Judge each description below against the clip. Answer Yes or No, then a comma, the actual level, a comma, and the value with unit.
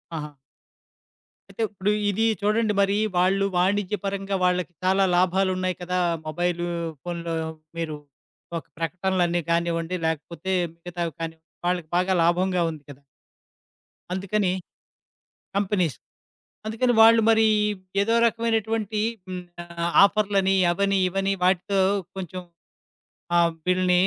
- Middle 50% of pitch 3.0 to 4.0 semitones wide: No, narrow, 2.5 semitones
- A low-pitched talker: No, medium, 185 Hz